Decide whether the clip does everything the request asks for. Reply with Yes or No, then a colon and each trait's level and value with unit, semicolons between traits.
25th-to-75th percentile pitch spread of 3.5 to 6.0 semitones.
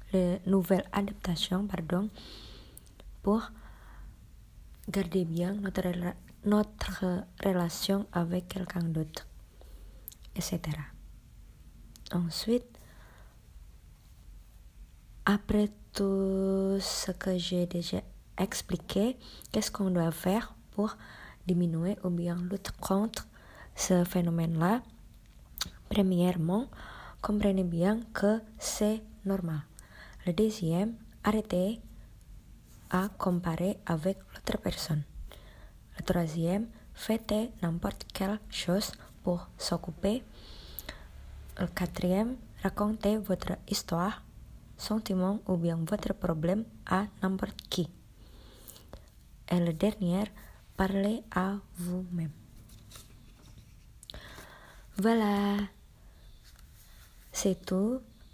No: average, 2.7 semitones